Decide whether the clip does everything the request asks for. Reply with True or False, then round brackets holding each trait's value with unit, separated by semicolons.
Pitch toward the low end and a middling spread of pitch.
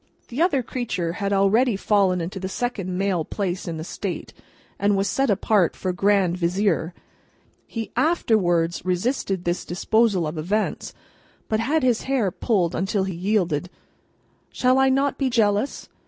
False (200 Hz; 4.4 semitones)